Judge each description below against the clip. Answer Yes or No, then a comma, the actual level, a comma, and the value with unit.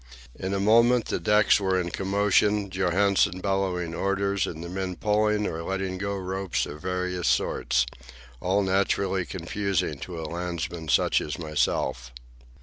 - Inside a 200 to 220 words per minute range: No, average, 145 wpm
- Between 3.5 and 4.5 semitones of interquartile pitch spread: No, narrow, 2.6 semitones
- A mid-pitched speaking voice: No, very low, 95 Hz